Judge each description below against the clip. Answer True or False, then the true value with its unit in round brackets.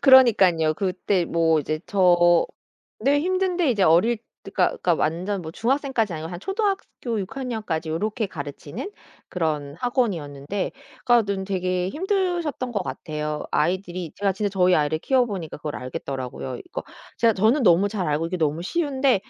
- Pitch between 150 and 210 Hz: True (190 Hz)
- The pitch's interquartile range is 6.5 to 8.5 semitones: True (6.8 semitones)